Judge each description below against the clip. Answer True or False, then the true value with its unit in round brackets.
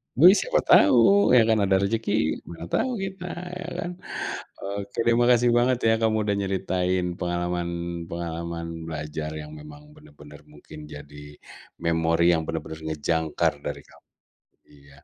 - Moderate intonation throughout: False (5.9 semitones)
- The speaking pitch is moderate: False (85 Hz)